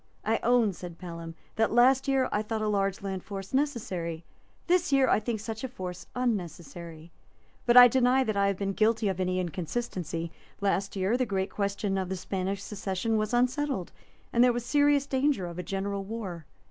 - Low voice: No, high, 200 Hz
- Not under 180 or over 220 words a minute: Yes, average, 190 wpm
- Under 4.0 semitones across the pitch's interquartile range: No, average, 4.7 semitones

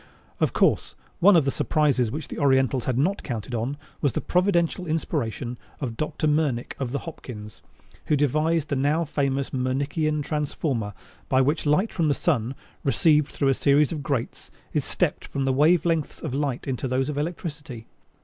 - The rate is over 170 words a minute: Yes, average, 180 wpm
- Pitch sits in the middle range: Yes, medium, 145 Hz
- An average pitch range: Yes, average, 3.0 semitones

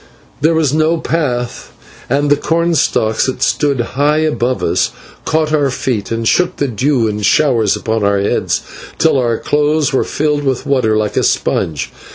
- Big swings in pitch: No, average, 5.0 semitones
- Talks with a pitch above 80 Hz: Yes, medium, 140 Hz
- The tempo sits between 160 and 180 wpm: Yes, average, 170 wpm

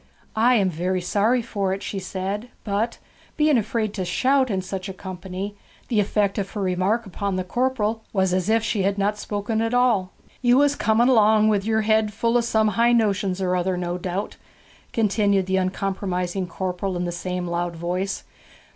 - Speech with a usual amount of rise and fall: Yes, average, 3.0 semitones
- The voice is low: No, high, 200 Hz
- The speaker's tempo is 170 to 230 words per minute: Yes, average, 190 wpm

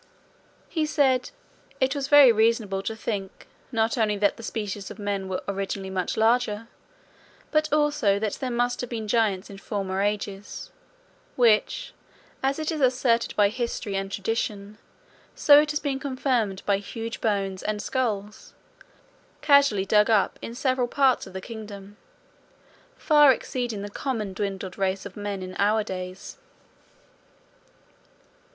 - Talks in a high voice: Yes, high, 215 Hz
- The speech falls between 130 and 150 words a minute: Yes, average, 145 wpm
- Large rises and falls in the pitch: No, average, 4.2 semitones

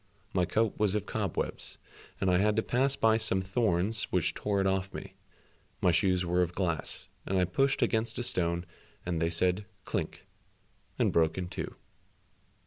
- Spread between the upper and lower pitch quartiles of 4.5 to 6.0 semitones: No, average, 3.4 semitones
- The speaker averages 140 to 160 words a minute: No, average, 175 wpm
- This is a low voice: Yes, very low, 95 Hz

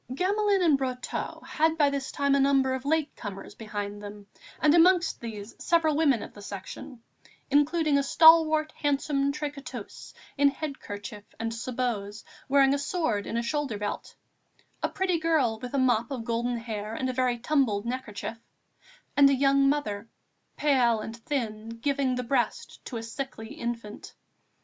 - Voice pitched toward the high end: Yes, very high, 260 Hz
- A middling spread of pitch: Yes, average, 4.3 semitones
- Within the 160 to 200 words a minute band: Yes, average, 165 wpm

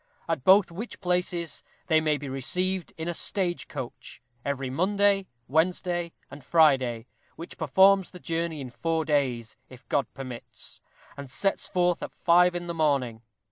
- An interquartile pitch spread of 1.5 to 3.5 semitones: No, average, 4.6 semitones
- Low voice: No, medium, 165 Hz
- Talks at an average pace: Yes, average, 155 wpm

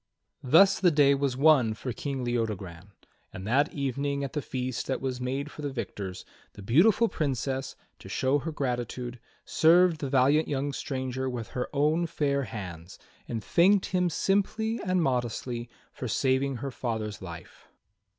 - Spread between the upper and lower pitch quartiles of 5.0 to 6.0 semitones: No, average, 3.8 semitones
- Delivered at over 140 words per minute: Yes, average, 160 wpm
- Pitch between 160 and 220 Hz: No, low, 135 Hz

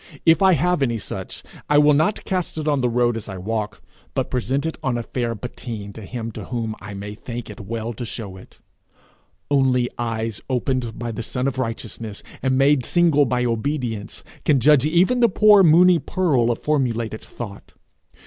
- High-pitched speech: No, low, 125 Hz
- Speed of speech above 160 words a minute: Yes, average, 190 wpm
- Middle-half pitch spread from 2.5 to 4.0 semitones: No, average, 4.6 semitones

